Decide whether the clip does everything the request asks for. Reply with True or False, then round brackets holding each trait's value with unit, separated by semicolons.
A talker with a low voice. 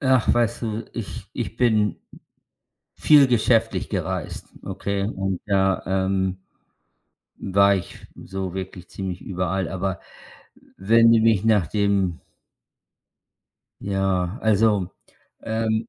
True (100 Hz)